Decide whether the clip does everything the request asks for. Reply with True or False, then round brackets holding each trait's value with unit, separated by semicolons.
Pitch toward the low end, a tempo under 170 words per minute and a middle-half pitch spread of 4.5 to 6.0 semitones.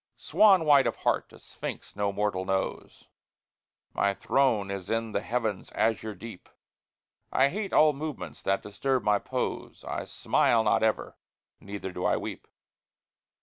True (110 Hz; 145 wpm; 5.2 semitones)